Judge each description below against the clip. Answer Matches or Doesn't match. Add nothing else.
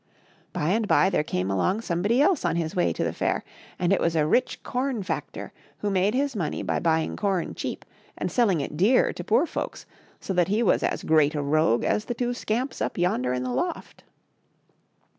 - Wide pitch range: Matches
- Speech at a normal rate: Doesn't match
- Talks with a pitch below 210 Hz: Matches